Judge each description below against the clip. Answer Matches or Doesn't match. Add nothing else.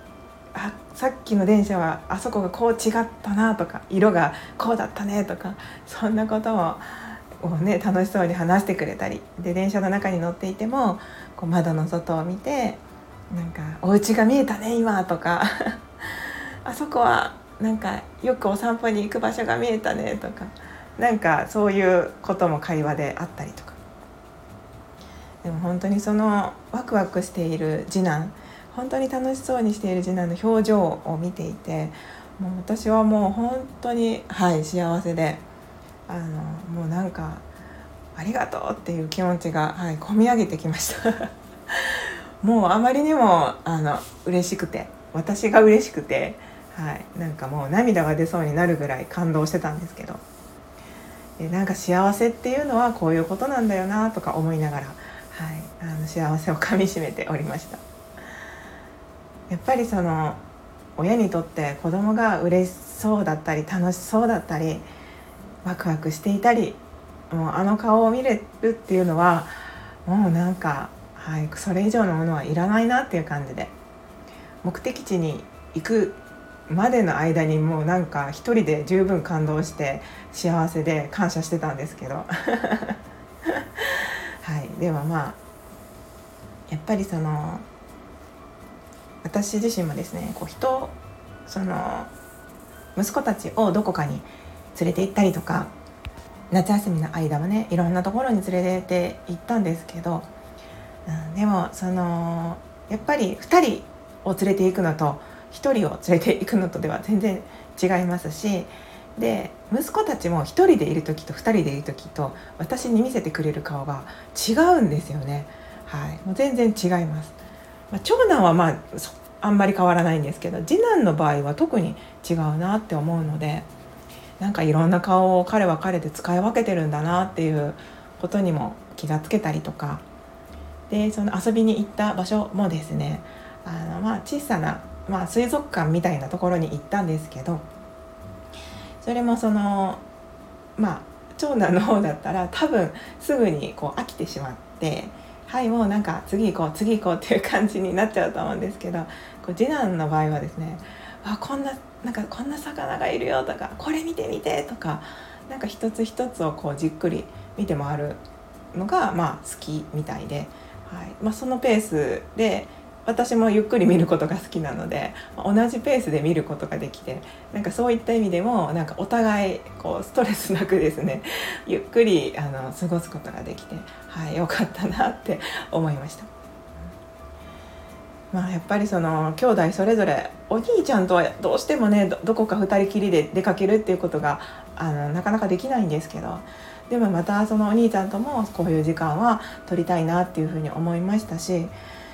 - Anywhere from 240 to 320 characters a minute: Matches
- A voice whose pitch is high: Doesn't match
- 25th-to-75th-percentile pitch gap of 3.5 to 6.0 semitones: Matches